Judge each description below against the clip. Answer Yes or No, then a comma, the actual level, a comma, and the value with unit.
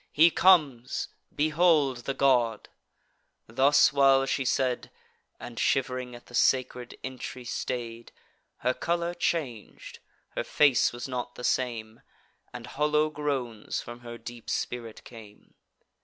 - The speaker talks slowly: Yes, slow, 125 wpm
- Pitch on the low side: Yes, low, 125 Hz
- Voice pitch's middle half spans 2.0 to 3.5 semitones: Yes, average, 3.2 semitones